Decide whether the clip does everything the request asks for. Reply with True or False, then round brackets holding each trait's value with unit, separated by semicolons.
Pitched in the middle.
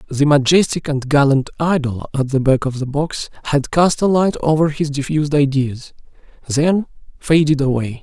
True (145 Hz)